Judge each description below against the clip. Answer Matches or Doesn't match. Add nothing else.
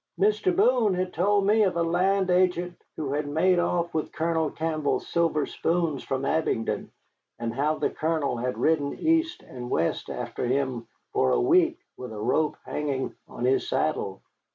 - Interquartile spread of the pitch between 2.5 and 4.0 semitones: Doesn't match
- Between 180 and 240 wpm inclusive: Doesn't match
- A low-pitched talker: Doesn't match